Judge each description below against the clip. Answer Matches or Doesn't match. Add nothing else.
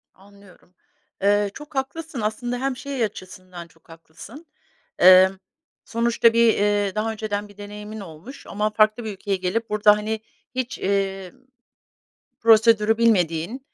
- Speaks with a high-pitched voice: Matches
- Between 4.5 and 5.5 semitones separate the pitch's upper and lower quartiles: Doesn't match